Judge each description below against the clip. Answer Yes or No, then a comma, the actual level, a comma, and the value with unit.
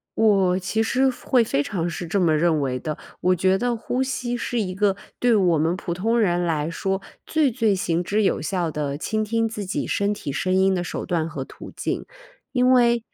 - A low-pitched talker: No, high, 190 Hz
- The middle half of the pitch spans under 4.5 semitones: No, average, 5.0 semitones